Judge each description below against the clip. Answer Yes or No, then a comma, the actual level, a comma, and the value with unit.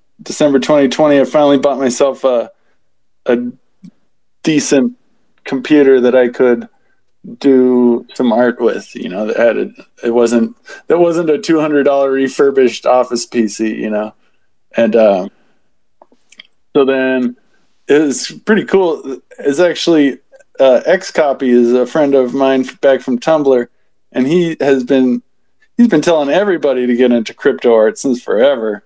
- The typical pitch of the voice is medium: No, low, 130 Hz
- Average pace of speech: Yes, average, 145 wpm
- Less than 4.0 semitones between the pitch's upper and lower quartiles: Yes, average, 2.7 semitones